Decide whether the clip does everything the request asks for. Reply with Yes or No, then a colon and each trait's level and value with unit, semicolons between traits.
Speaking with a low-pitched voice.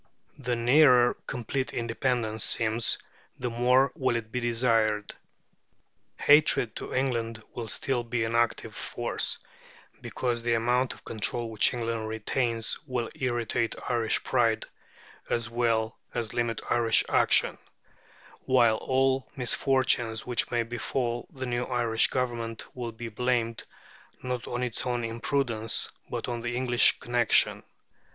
Yes: low, 120 Hz